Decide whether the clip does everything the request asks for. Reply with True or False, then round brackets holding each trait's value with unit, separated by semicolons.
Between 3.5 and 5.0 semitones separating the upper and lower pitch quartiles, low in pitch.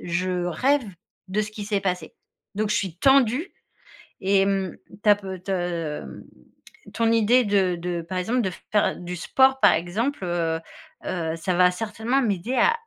False (4.0 semitones; 195 Hz)